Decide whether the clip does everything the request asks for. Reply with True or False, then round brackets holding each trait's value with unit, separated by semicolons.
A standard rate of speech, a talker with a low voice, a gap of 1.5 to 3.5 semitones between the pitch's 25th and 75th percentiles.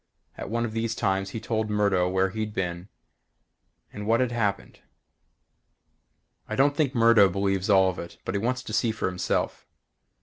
True (175 wpm; 105 Hz; 3.2 semitones)